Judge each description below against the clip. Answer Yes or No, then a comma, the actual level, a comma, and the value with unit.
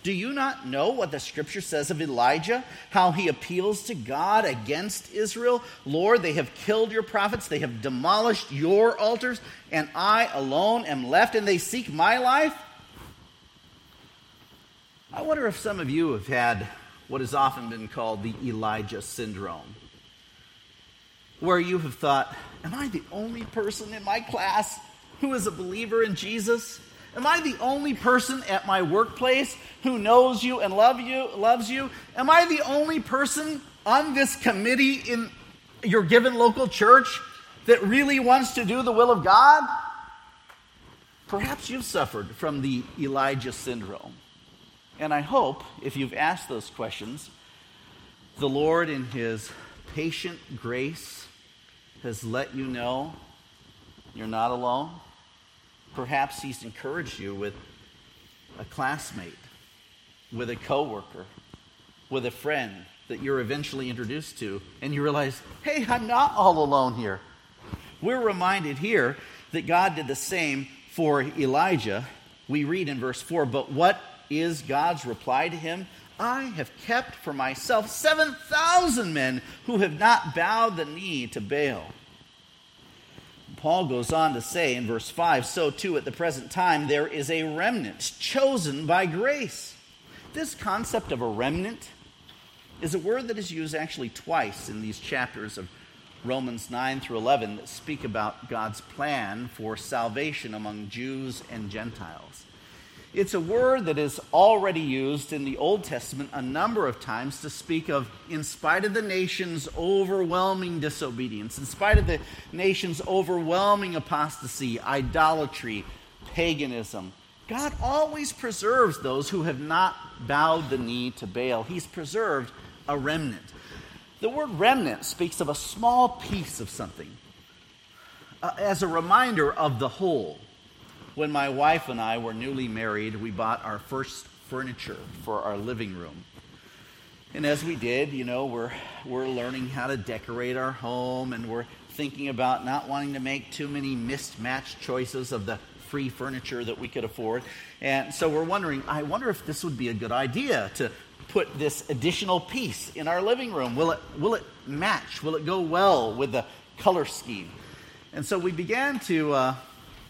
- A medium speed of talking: Yes, average, 155 wpm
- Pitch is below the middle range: No, medium, 150 Hz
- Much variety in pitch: Yes, wide, 8.7 semitones